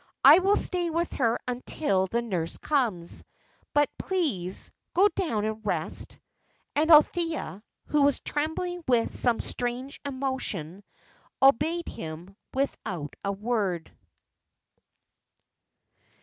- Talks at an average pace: No, slow, 105 wpm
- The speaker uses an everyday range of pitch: No, wide, 7.7 semitones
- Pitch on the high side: Yes, very high, 250 Hz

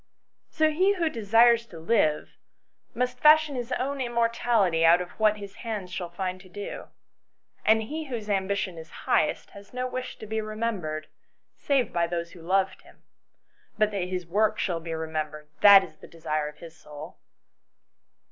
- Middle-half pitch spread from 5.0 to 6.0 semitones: Yes, wide, 5.6 semitones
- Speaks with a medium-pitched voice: No, high, 200 Hz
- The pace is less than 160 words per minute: No, average, 170 wpm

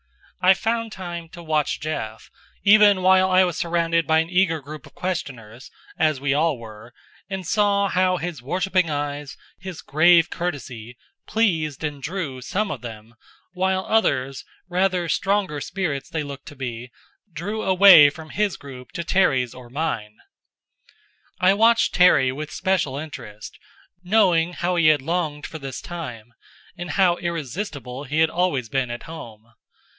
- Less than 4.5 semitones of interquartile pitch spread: No, average, 5.2 semitones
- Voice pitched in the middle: Yes, medium, 160 Hz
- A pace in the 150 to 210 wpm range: Yes, average, 155 wpm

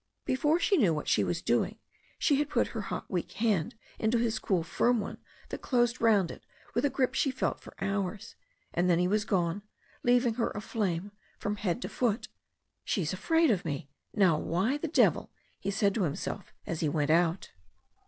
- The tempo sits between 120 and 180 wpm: No, average, 200 wpm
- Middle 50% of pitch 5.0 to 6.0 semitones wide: Yes, wide, 5.4 semitones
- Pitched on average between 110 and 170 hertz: No, high, 205 Hz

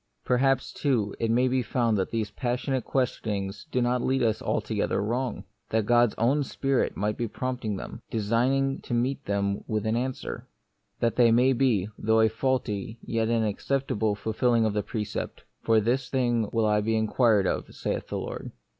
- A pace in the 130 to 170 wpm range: No, average, 195 wpm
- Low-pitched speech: Yes, low, 115 Hz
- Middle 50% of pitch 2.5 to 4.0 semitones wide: Yes, average, 2.9 semitones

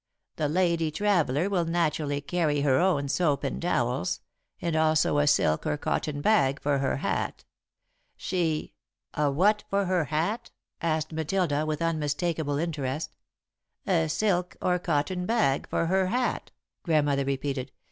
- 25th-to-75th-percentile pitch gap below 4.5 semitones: Yes, average, 3.6 semitones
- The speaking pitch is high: No, medium, 155 Hz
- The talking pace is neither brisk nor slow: Yes, average, 145 wpm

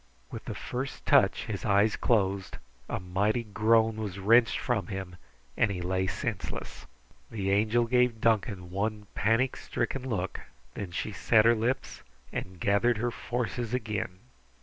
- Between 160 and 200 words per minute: No, average, 150 wpm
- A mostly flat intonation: No, average, 3.2 semitones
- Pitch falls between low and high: No, low, 110 Hz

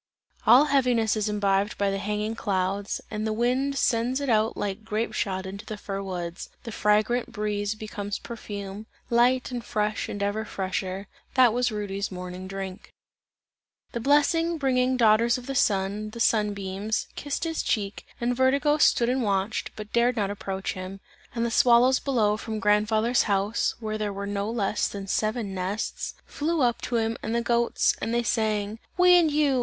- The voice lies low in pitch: No, high, 215 Hz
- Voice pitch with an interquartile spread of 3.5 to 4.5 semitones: No, average, 3.1 semitones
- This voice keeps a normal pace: Yes, average, 180 wpm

